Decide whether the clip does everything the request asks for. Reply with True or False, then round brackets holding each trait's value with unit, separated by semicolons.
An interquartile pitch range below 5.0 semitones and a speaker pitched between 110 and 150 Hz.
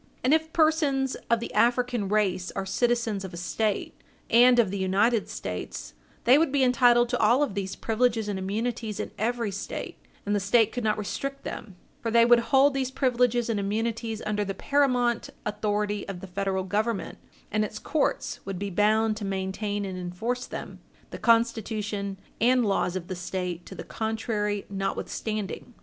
False (3.5 semitones; 215 Hz)